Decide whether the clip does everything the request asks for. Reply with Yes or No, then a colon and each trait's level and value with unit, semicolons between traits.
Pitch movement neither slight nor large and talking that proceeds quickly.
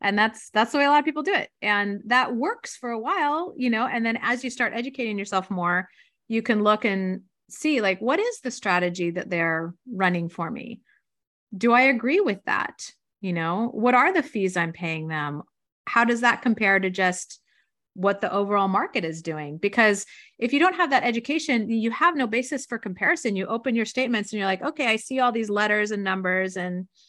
Yes: average, 4.9 semitones; fast, 215 wpm